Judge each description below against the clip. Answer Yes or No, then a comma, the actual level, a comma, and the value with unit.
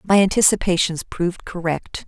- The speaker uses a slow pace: Yes, slow, 115 wpm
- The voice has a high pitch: No, medium, 180 Hz